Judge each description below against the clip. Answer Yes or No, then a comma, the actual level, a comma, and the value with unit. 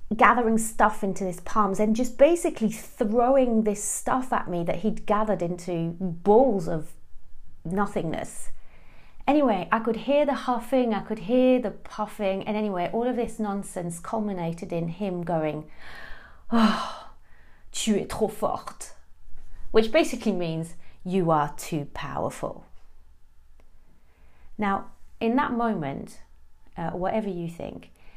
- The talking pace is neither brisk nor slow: No, slow, 130 wpm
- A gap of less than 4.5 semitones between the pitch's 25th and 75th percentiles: No, average, 5.3 semitones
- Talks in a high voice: Yes, high, 200 Hz